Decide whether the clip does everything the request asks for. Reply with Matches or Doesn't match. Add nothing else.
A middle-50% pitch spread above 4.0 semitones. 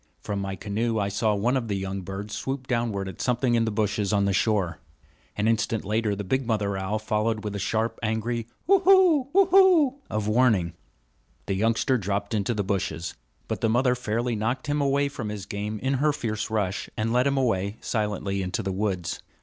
Doesn't match